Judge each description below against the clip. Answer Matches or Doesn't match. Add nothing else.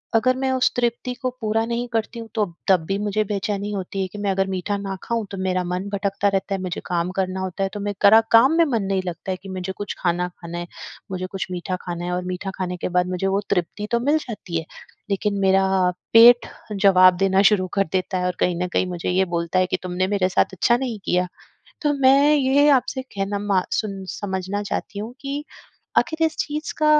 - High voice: Matches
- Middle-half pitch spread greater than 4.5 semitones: Doesn't match